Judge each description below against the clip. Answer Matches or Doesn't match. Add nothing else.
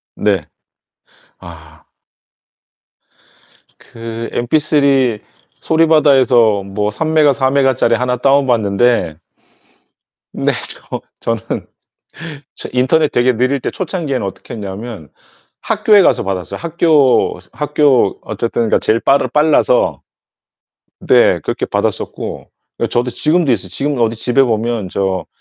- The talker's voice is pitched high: Doesn't match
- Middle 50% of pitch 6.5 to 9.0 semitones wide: Doesn't match